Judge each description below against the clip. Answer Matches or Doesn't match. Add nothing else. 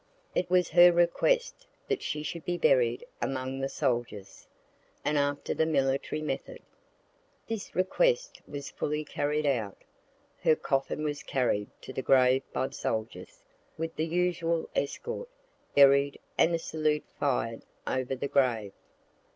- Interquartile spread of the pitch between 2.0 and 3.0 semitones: Doesn't match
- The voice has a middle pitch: Matches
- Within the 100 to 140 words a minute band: Matches